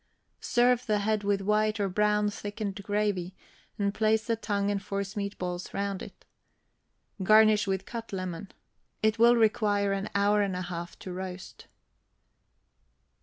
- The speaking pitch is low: No, high, 205 Hz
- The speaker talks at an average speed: Yes, average, 145 wpm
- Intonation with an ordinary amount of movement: No, narrow, 1.7 semitones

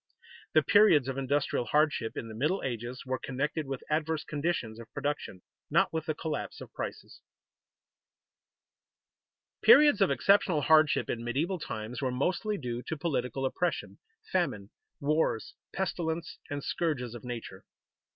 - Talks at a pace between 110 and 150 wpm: Yes, average, 140 wpm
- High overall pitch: No, medium, 145 Hz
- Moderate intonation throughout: Yes, average, 4.4 semitones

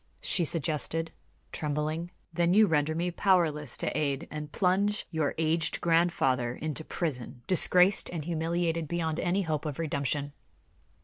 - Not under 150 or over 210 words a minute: No, slow, 135 wpm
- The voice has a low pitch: No, medium, 160 Hz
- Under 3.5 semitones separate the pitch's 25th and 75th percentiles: Yes, narrow, 2.5 semitones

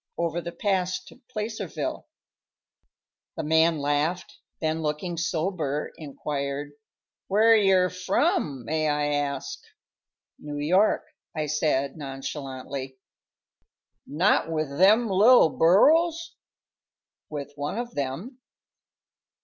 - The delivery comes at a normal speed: No, slow, 100 wpm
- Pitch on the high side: No, medium, 160 Hz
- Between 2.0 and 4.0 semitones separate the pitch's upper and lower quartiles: No, average, 4.7 semitones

